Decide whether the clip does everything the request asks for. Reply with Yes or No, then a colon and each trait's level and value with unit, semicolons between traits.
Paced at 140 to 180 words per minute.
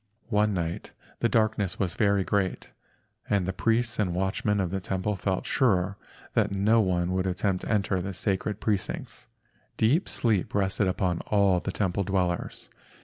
Yes: average, 160 wpm